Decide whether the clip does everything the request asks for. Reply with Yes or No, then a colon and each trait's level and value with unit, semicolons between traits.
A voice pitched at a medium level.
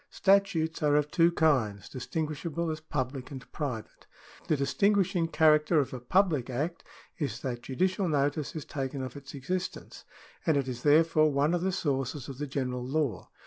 Yes: medium, 150 Hz